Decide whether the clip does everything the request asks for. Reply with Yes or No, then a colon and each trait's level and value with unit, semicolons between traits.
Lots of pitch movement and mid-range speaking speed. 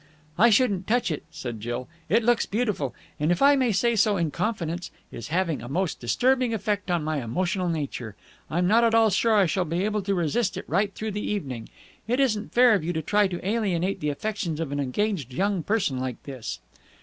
No: wide, 5.9 semitones; fast, 215 wpm